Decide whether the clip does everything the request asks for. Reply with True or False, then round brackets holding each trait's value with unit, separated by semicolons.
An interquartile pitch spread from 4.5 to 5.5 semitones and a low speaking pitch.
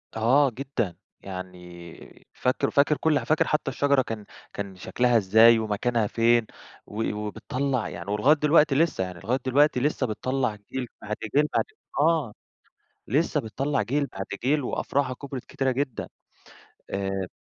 True (5.1 semitones; 125 Hz)